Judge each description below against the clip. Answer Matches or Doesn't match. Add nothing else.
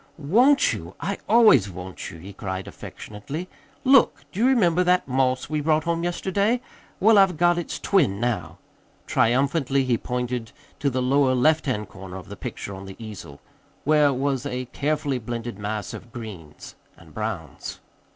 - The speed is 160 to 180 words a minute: Matches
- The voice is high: Doesn't match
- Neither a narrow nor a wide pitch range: Doesn't match